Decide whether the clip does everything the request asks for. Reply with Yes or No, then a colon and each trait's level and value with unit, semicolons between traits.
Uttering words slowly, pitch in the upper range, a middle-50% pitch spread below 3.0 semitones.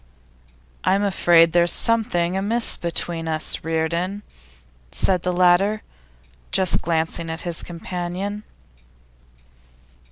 No: slow, 95 wpm; medium, 175 Hz; narrow, 2.6 semitones